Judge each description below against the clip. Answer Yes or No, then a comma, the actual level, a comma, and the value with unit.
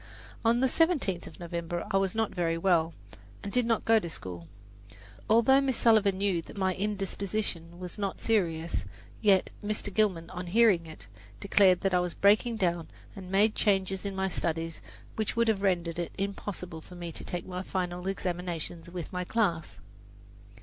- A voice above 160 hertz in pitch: Yes, high, 190 Hz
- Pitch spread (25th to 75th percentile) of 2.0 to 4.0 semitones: Yes, average, 3.3 semitones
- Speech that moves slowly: No, average, 175 wpm